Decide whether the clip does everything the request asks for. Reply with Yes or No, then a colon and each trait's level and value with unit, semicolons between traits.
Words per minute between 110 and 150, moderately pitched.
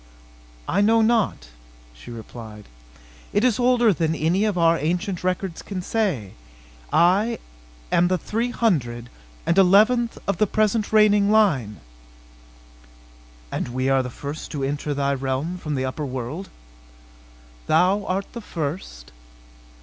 Yes: slow, 135 wpm; medium, 180 Hz